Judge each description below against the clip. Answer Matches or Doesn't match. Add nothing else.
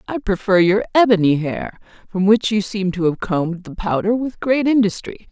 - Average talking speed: Matches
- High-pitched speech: Matches